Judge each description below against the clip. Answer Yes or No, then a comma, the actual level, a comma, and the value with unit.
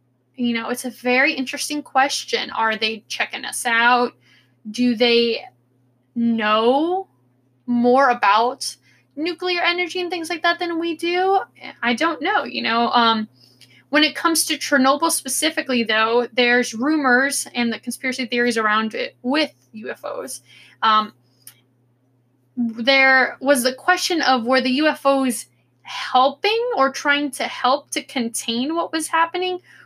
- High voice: Yes, very high, 255 Hz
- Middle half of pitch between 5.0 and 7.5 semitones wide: Yes, average, 5.3 semitones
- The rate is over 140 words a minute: No, slow, 135 wpm